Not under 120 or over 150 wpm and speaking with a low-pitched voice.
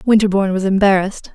No: slow, 135 wpm; high, 195 Hz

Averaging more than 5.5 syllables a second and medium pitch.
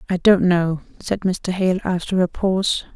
No: 4.5 syllables/s; medium, 180 Hz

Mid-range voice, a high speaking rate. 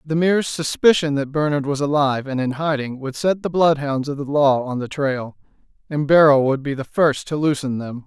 Yes: medium, 145 Hz; fast, 215 wpm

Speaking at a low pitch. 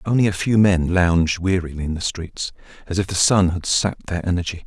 Yes: very low, 90 Hz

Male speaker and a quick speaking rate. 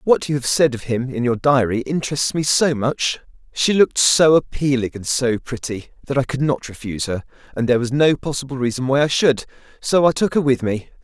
Yes: male; fast, 225 wpm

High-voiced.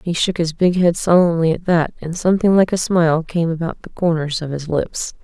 No: medium, 170 Hz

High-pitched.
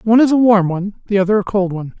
Yes: high, 200 Hz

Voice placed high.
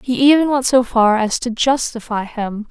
Yes: high, 240 Hz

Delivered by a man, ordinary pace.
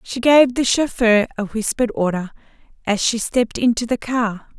No: female; average, 170 wpm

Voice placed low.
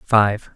Yes: low, 105 Hz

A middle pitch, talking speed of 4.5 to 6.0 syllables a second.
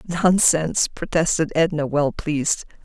Yes: medium, 160 Hz; 5.3 syllables/s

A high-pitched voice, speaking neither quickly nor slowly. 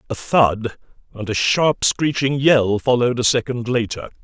No: low, 120 Hz; average, 155 wpm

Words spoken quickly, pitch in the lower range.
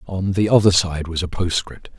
Yes: fast, 210 wpm; very low, 90 Hz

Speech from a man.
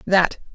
No: female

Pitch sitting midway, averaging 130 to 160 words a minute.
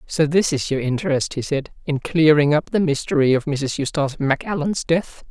No: medium, 150 Hz; average, 190 wpm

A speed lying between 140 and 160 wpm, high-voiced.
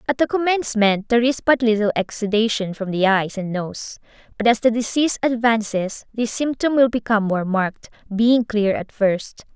No: average, 175 wpm; high, 225 Hz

